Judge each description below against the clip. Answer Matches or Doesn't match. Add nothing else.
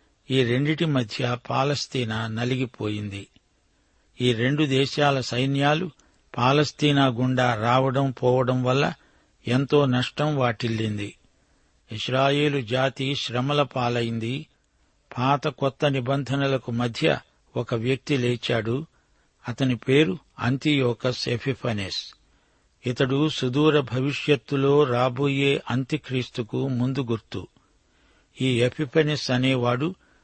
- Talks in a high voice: Doesn't match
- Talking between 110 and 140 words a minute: Doesn't match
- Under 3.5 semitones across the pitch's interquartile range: Matches